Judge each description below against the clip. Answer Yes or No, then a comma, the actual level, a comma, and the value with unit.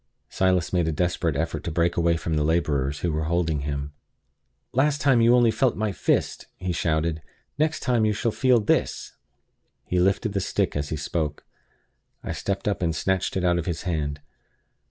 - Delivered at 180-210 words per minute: Yes, average, 190 wpm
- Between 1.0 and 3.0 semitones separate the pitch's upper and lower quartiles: No, average, 4.5 semitones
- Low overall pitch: Yes, very low, 85 Hz